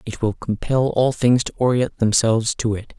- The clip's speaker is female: No, male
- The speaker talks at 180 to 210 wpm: Yes, average, 200 wpm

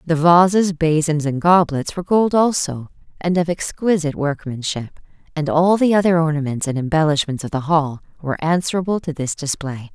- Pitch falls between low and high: Yes, medium, 160 Hz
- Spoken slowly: No, average, 165 wpm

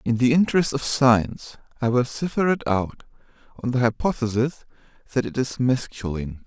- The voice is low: Yes, low, 125 Hz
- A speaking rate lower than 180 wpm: Yes, average, 160 wpm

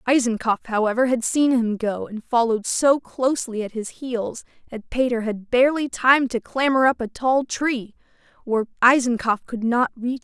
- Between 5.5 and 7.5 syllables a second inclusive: No, 5.0 syllables/s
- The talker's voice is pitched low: No, high, 240 Hz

